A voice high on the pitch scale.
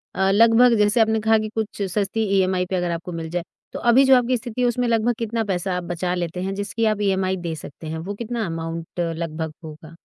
Yes: high, 195 Hz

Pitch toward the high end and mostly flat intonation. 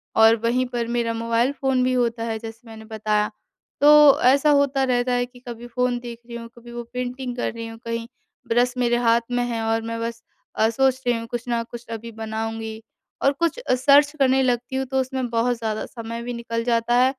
Yes: high, 240 Hz; narrow, 1.8 semitones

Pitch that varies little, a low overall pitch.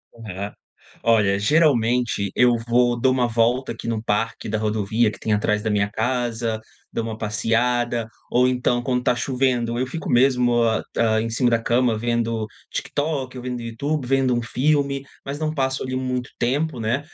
Yes: narrow, 2.3 semitones; low, 120 Hz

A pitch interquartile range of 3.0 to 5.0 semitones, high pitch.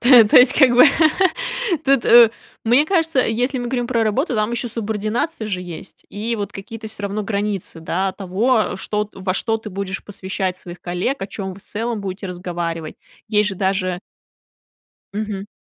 Yes: average, 3.7 semitones; high, 210 Hz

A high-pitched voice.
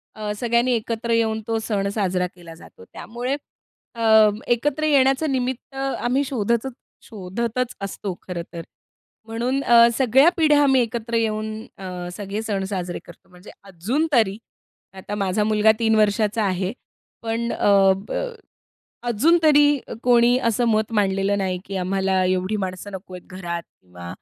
Yes: high, 215 Hz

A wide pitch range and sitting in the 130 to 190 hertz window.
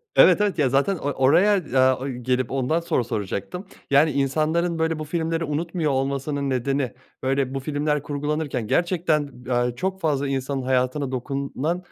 No: average, 3.6 semitones; medium, 140 Hz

